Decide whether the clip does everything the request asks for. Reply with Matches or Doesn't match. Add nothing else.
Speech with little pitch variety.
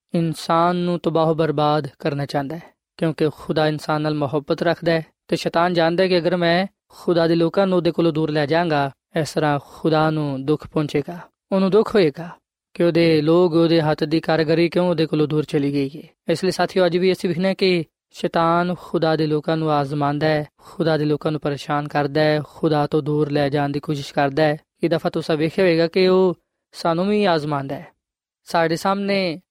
Matches